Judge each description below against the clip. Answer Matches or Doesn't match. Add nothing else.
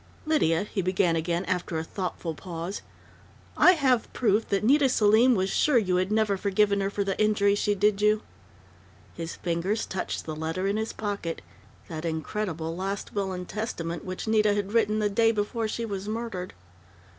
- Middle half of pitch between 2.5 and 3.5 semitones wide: Matches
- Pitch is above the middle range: Matches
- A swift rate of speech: Doesn't match